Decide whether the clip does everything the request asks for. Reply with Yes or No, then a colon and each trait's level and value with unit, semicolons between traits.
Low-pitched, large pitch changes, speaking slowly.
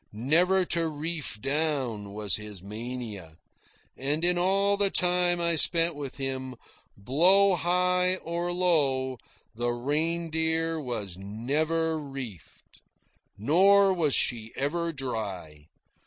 No: medium, 150 Hz; wide, 6.2 semitones; slow, 110 wpm